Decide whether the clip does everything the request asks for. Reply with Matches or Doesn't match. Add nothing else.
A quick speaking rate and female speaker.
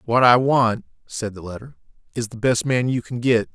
Doesn't match